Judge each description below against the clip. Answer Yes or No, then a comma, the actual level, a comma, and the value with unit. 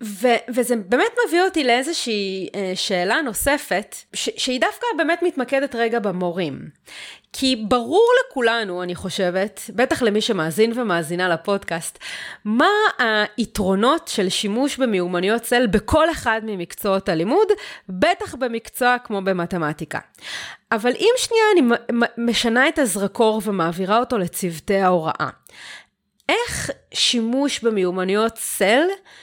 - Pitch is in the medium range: No, high, 230 Hz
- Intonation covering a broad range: Yes, wide, 6.1 semitones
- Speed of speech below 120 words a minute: Yes, average, 110 wpm